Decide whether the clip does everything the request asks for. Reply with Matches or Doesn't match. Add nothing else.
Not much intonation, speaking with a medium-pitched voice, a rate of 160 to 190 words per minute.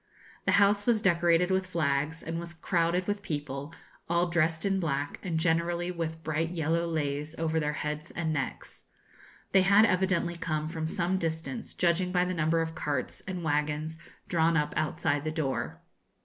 Matches